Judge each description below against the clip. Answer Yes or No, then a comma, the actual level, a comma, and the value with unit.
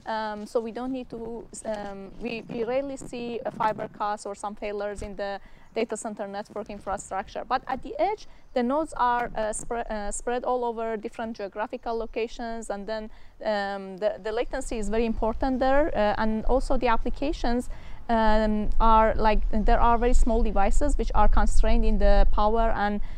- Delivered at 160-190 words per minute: Yes, average, 180 wpm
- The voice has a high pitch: Yes, high, 225 Hz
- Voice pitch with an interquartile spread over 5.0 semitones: No, narrow, 2.4 semitones